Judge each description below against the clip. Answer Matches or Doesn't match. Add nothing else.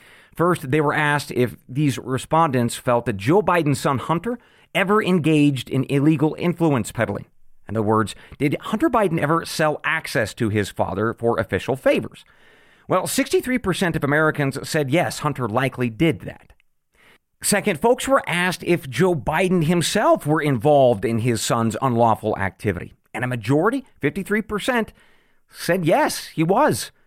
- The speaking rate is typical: Matches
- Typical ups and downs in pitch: Doesn't match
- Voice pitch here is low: Doesn't match